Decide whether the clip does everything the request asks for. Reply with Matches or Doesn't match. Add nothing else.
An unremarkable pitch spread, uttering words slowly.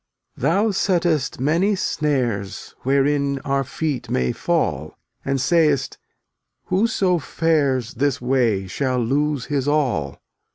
Matches